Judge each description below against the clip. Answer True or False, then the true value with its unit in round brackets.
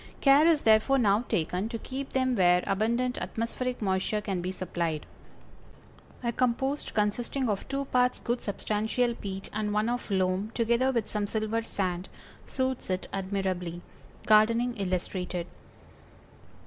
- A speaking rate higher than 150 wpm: False (135 wpm)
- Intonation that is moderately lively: True (4.4 semitones)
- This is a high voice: True (215 Hz)